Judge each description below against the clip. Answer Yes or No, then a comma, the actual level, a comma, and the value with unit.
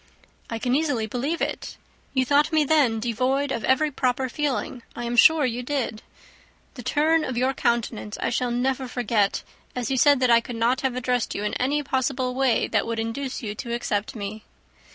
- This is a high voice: Yes, very high, 250 Hz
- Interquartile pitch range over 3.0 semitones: No, narrow, 2.6 semitones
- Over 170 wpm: Yes, average, 195 wpm